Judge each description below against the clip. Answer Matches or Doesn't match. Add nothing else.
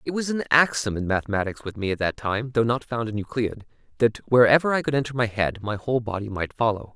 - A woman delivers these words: Doesn't match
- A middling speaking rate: Doesn't match